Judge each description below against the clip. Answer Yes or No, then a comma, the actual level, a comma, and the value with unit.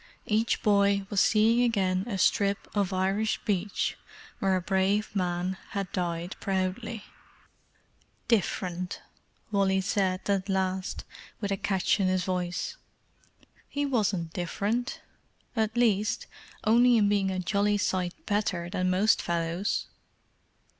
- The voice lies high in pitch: Yes, high, 195 Hz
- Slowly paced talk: Yes, slow, 120 wpm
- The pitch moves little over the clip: Yes, narrow, 2.3 semitones